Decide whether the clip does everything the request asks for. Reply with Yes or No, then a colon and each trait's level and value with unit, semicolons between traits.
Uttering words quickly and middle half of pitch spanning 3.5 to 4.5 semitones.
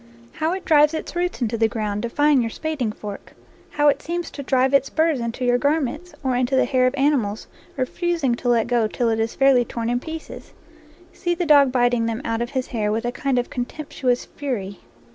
Yes: fast, 220 wpm; average, 4.0 semitones